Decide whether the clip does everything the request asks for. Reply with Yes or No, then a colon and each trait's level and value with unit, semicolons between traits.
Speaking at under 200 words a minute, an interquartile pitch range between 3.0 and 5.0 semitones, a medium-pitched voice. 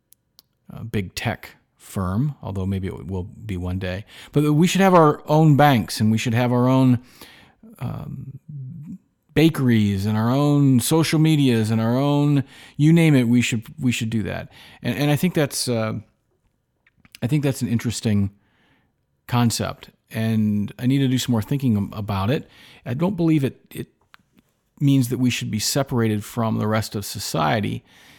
No: average, 170 wpm; average, 4.7 semitones; low, 125 Hz